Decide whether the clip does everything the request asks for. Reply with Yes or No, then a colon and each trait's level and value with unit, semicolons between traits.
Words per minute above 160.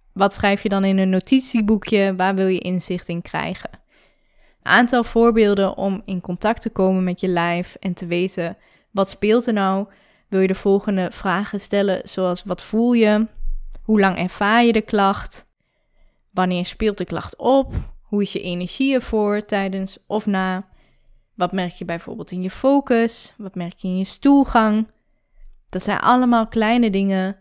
Yes: average, 170 wpm